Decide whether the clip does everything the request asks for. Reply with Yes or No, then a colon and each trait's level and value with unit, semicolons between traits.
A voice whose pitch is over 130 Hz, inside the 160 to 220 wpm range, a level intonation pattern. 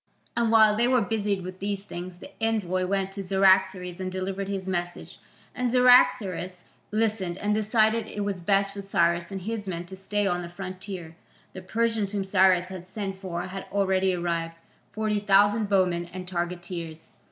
Yes: high, 190 Hz; average, 175 wpm; narrow, 2.3 semitones